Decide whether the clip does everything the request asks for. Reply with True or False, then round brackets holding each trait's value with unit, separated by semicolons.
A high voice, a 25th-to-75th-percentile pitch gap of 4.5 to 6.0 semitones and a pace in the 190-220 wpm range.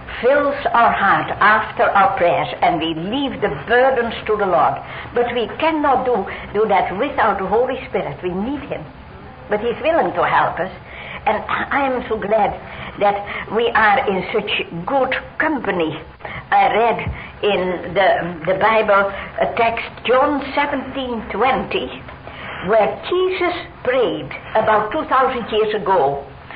False (230 Hz; 5.1 semitones; 140 wpm)